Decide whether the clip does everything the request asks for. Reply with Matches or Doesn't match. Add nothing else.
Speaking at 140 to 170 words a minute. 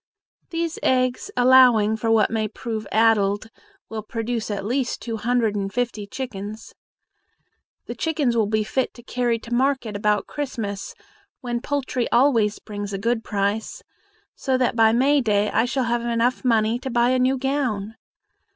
Matches